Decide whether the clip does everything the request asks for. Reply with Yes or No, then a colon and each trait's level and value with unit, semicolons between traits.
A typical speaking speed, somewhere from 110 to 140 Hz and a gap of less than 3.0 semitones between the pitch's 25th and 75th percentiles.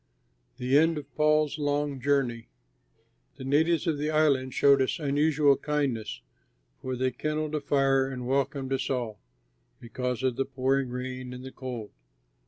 Yes: average, 155 wpm; low, 135 Hz; narrow, 2.5 semitones